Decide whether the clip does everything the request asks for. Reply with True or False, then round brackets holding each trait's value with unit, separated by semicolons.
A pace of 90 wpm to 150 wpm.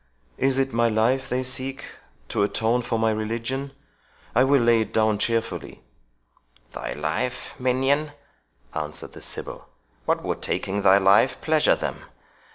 True (145 wpm)